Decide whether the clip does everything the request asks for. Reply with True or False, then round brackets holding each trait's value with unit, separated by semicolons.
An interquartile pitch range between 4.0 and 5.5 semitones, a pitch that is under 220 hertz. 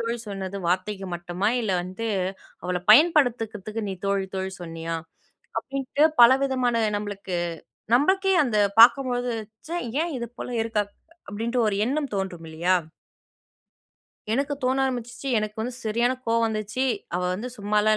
False (4.4 semitones; 225 Hz)